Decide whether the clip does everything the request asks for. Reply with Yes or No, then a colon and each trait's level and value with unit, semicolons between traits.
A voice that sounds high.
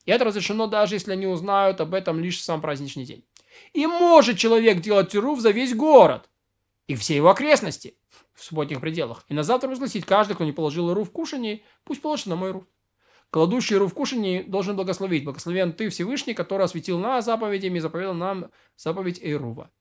Yes: high, 195 Hz